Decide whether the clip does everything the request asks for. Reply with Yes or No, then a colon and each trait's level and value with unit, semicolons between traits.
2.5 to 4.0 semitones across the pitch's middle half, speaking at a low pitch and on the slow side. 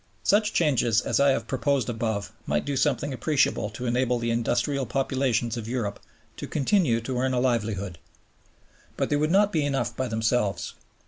No: average, 3.4 semitones; low, 125 Hz; average, 175 wpm